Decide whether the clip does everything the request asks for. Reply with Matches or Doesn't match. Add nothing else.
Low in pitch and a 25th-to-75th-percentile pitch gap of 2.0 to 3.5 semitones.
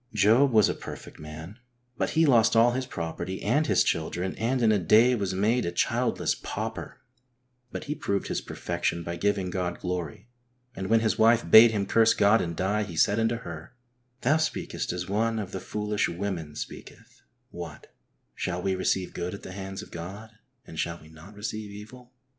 Doesn't match